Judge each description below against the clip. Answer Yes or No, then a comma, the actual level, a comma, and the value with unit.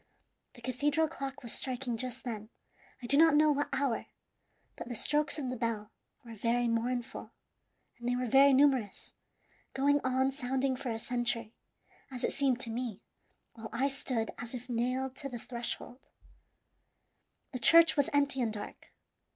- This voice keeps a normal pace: Yes, average, 165 wpm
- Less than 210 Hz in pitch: No, very high, 255 Hz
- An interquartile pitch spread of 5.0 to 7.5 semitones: No, average, 2.7 semitones